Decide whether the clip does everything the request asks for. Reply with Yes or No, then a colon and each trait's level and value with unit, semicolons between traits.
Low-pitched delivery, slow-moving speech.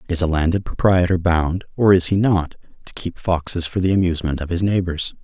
No: very low, 90 Hz; fast, 205 wpm